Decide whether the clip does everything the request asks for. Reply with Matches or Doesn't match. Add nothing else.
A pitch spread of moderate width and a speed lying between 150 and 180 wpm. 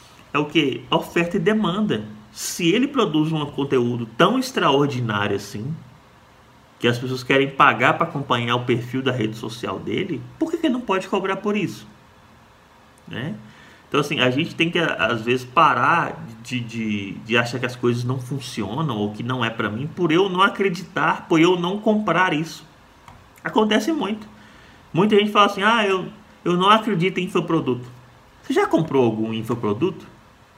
Doesn't match